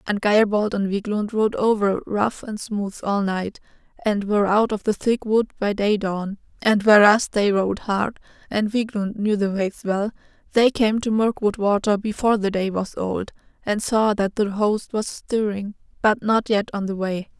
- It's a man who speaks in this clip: No, female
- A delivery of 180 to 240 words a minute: Yes, average, 190 wpm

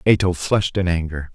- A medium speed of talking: Yes, average, 180 wpm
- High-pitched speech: No, very low, 90 Hz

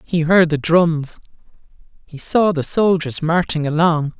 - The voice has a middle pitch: Yes, medium, 165 Hz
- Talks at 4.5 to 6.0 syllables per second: No, 4.0 syllables/s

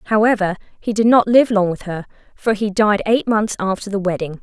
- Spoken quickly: Yes, fast, 215 wpm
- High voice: Yes, high, 205 Hz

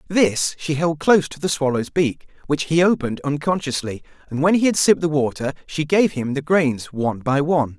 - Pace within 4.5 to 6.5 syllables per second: Yes, 5.5 syllables/s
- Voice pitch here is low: No, medium, 150 Hz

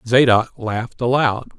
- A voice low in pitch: Yes, low, 120 Hz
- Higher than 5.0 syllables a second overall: No, 4.4 syllables/s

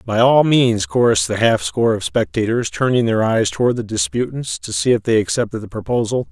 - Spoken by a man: Yes, male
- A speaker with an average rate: No, fast, 210 wpm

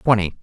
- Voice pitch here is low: Yes, low, 105 Hz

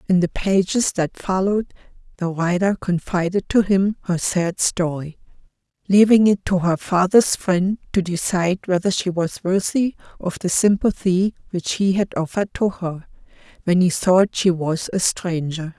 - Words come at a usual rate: Yes, average, 155 wpm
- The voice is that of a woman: Yes, female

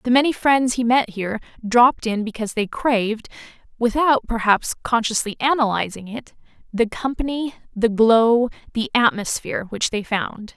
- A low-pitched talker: No, high, 230 Hz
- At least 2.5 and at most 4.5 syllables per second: No, 4.9 syllables/s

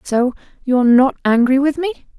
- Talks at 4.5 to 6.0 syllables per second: Yes, 5.0 syllables/s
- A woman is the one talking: Yes, female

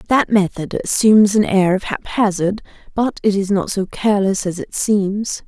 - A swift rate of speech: No, average, 175 wpm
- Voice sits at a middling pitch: No, high, 200 Hz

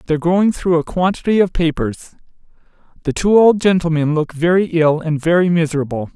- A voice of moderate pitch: Yes, medium, 165 Hz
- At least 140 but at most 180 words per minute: Yes, average, 165 wpm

